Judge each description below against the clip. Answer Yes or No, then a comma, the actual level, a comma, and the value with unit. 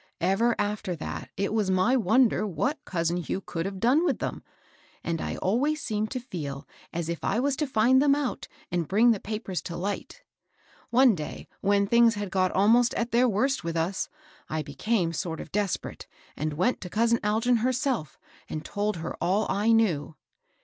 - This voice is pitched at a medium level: No, high, 210 Hz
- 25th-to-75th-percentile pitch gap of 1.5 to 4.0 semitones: No, average, 5.2 semitones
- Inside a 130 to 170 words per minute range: No, average, 185 wpm